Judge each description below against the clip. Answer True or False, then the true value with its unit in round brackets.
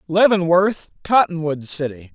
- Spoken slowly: True (85 wpm)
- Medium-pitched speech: True (170 Hz)